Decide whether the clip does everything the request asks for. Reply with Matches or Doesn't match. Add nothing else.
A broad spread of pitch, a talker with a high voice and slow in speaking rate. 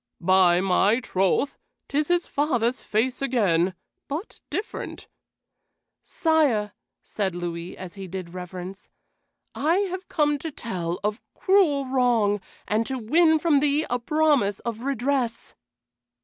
Matches